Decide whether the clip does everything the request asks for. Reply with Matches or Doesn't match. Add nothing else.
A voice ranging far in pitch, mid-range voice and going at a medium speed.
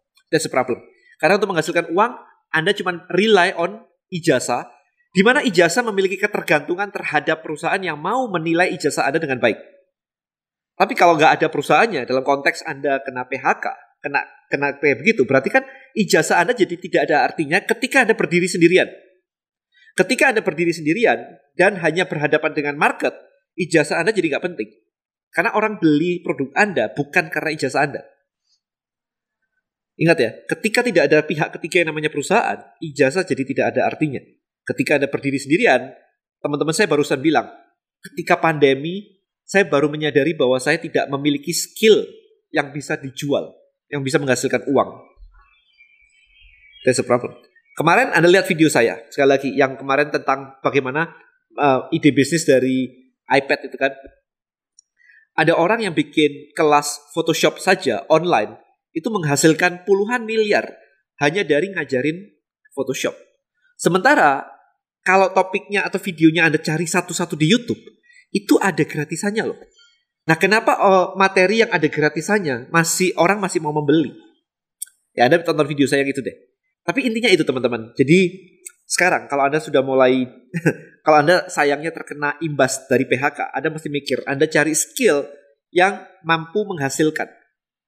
Doesn't match